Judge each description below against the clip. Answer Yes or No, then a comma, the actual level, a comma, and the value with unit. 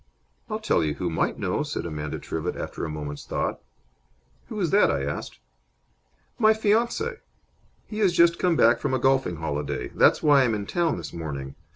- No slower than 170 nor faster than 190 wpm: Yes, average, 185 wpm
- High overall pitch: No, low, 115 Hz